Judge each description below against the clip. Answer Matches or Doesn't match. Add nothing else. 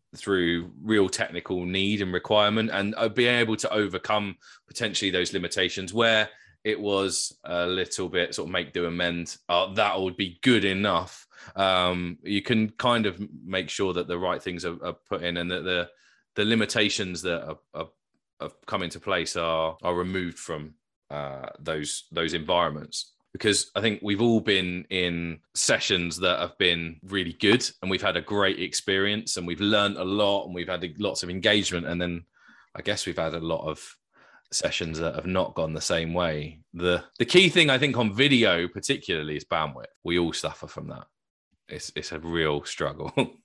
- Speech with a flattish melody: Doesn't match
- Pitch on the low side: Matches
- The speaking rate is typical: Matches